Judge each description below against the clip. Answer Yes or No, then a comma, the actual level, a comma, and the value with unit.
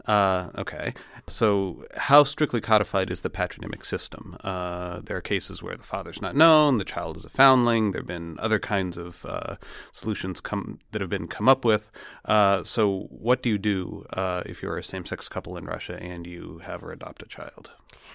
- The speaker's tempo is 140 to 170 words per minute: No, average, 200 wpm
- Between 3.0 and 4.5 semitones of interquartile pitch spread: Yes, average, 3.7 semitones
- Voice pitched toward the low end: Yes, low, 100 Hz